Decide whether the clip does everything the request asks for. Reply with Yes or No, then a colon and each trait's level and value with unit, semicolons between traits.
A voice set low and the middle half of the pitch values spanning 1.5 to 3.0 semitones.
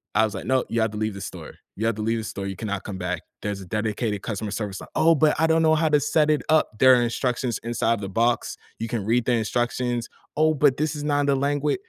No: low, 115 Hz; average, 5.2 semitones